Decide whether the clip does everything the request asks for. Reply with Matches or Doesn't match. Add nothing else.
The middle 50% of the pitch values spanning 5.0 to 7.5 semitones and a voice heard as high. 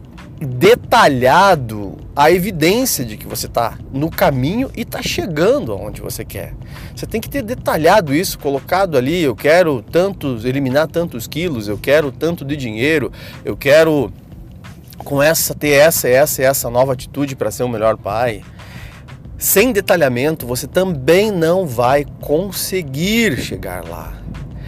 Doesn't match